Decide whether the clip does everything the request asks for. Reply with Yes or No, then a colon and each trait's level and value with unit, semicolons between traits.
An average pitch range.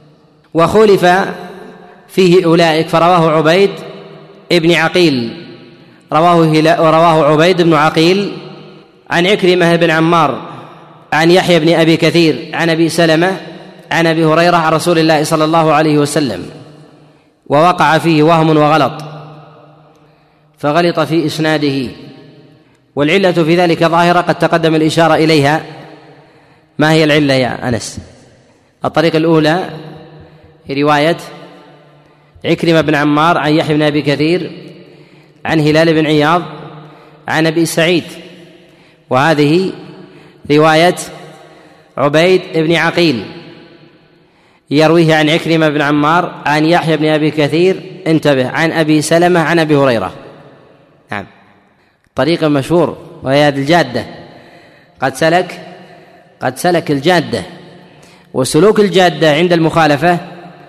No: narrow, 1.8 semitones